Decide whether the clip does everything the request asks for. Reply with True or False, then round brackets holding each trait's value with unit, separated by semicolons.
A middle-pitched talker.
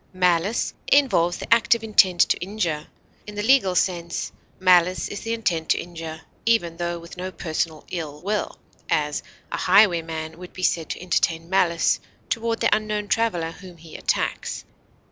True (180 Hz)